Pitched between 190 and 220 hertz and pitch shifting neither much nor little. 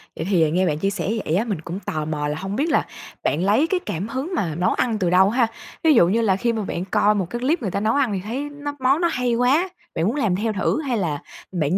No: high, 205 Hz; wide, 6.1 semitones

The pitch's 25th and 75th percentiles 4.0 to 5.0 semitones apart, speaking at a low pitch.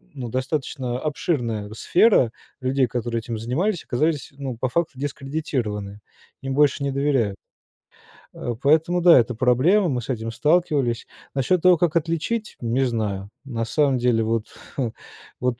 Yes: average, 4.5 semitones; low, 130 Hz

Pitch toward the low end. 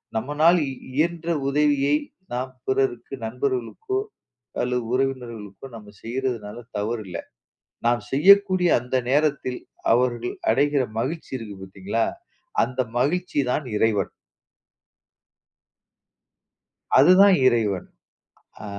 Yes: low, 130 Hz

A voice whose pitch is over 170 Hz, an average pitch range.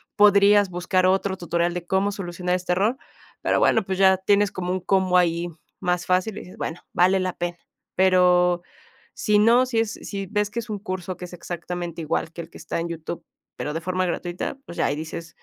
No: medium, 185 Hz; narrow, 2.1 semitones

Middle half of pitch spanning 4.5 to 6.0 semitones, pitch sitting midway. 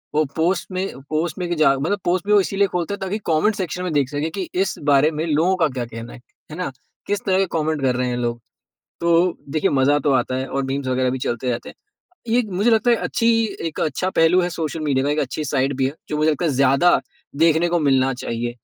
Yes: average, 5.0 semitones; medium, 155 Hz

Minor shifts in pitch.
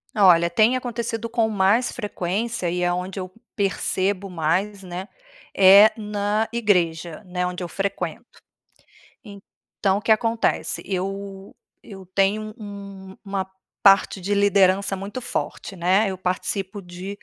Yes: narrow, 2.1 semitones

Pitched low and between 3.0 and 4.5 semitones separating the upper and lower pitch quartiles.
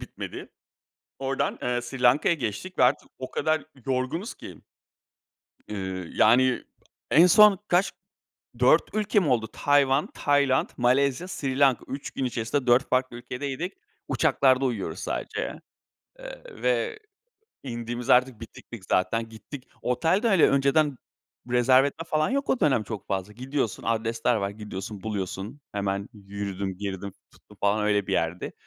No: low, 125 Hz; average, 5.2 semitones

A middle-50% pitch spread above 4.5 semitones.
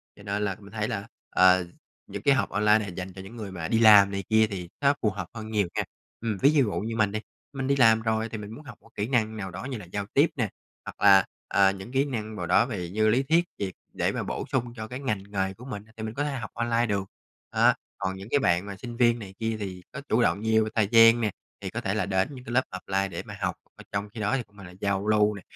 No: average, 3.1 semitones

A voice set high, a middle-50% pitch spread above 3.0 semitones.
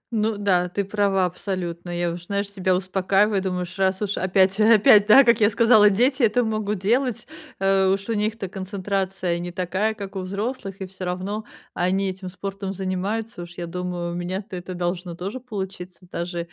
No: high, 195 Hz; narrow, 2.4 semitones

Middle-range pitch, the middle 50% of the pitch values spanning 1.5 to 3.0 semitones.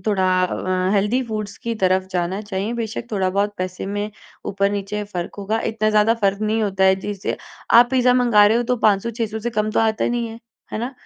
No: high, 210 Hz; narrow, 2.4 semitones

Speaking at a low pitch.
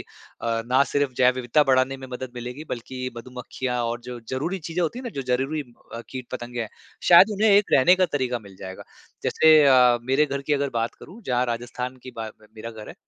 Yes: low, 130 Hz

